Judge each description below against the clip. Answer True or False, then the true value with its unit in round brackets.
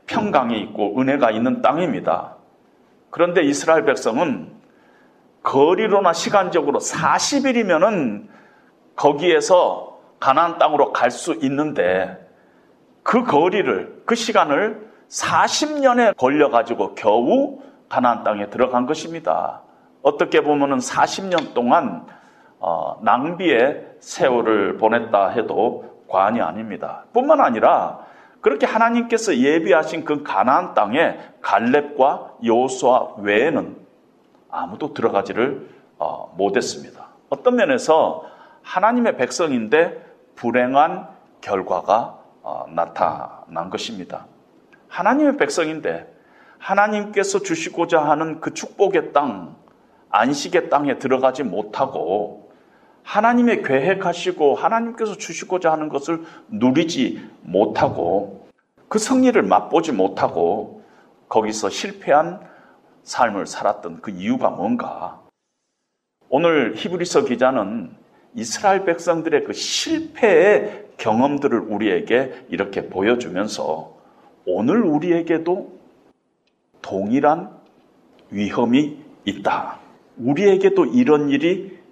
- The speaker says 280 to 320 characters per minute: False (240 characters per minute)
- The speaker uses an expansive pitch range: True (8.9 semitones)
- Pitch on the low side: False (195 Hz)